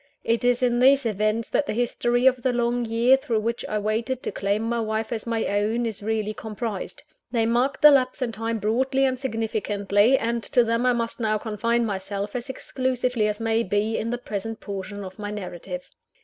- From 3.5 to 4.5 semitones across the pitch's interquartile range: No, narrow, 2.4 semitones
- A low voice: No, high, 230 Hz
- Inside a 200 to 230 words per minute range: Yes, fast, 205 wpm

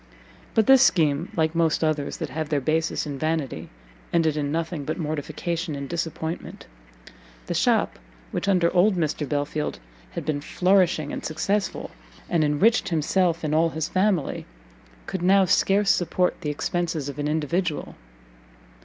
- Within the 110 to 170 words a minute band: Yes, average, 150 wpm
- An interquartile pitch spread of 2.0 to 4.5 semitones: Yes, average, 3.2 semitones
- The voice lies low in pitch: No, medium, 160 Hz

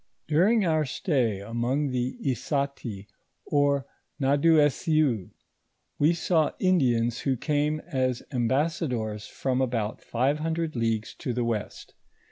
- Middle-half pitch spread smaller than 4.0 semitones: No, average, 4.5 semitones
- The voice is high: No, low, 135 Hz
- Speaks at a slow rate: Yes, slow, 110 wpm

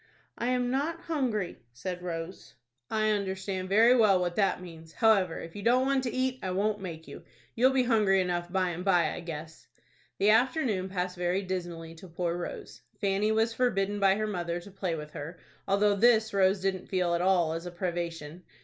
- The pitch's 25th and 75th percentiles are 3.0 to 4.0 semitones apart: Yes, average, 3.7 semitones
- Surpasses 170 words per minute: Yes, average, 195 wpm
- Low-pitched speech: No, high, 190 Hz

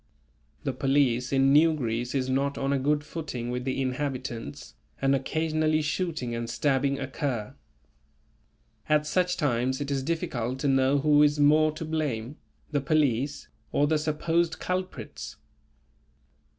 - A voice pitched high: No, medium, 140 Hz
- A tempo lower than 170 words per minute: Yes, average, 140 wpm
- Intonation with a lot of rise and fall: No, average, 2.9 semitones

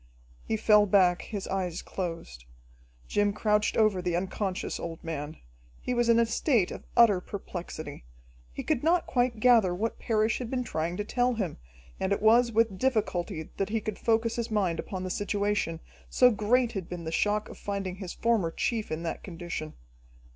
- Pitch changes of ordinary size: Yes, average, 4.3 semitones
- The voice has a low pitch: No, high, 205 Hz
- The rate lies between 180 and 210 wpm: Yes, average, 185 wpm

